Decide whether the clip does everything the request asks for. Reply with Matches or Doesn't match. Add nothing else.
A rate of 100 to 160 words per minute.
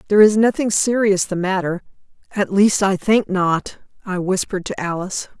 Matches